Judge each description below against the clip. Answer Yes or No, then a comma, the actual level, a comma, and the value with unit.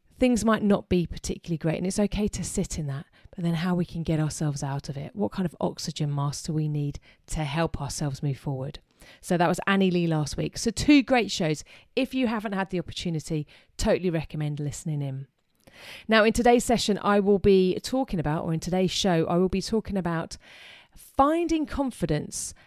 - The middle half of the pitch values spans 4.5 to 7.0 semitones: Yes, average, 4.9 semitones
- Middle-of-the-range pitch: Yes, medium, 175 Hz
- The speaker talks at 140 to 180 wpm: No, fast, 205 wpm